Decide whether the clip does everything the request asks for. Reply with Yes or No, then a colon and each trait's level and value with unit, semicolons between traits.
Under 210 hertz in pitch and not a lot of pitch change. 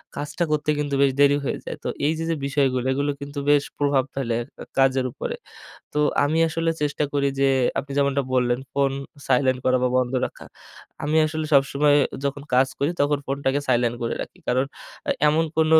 Yes: medium, 140 Hz; narrow, 1.8 semitones